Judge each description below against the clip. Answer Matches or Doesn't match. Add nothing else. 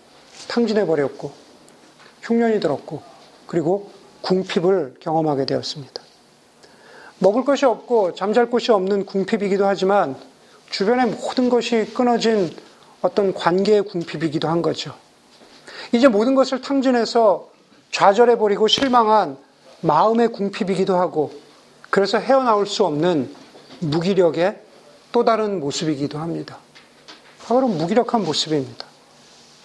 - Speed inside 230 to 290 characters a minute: Matches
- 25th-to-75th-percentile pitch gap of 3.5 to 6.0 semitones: Matches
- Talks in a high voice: Matches